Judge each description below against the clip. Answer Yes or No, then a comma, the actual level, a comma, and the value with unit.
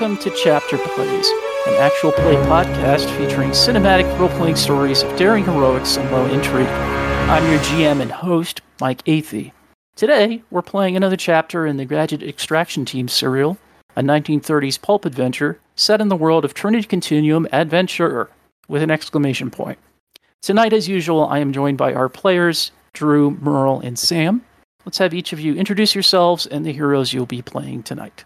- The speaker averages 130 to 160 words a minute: No, average, 170 wpm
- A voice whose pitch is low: No, medium, 155 Hz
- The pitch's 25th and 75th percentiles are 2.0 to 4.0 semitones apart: No, average, 5.3 semitones